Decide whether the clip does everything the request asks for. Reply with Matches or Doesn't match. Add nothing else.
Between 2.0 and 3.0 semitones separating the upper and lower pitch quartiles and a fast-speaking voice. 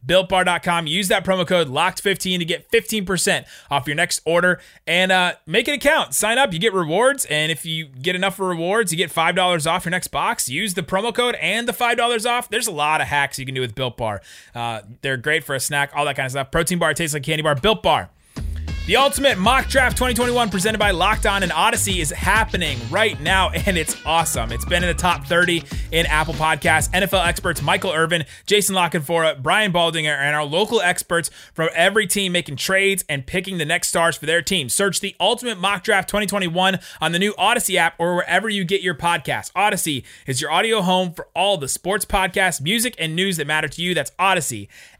Doesn't match